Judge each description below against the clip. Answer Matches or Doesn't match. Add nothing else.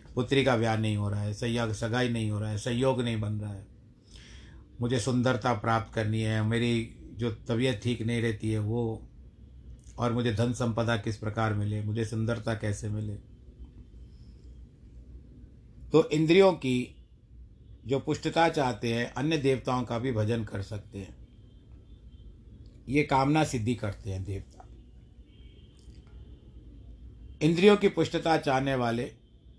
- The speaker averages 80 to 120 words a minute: Doesn't match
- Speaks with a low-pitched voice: Matches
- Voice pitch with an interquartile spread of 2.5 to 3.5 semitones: Matches